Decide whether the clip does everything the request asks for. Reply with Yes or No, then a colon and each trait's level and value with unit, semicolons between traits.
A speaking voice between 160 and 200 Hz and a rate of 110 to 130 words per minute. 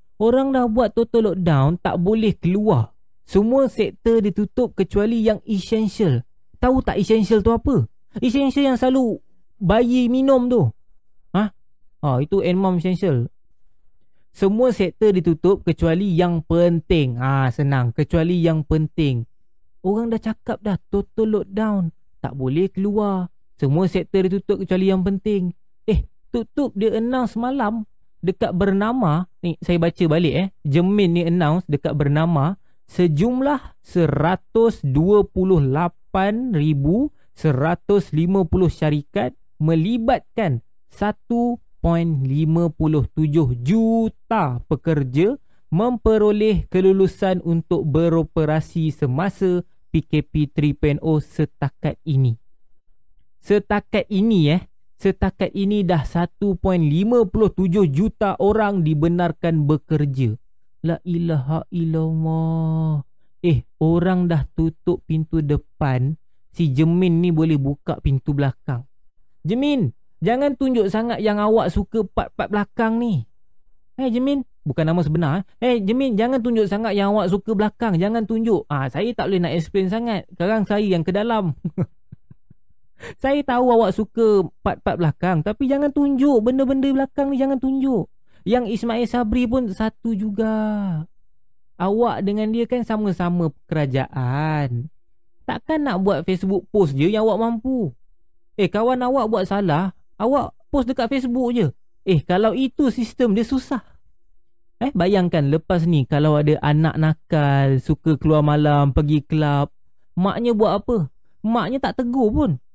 Yes: medium, 185 Hz; average, 120 wpm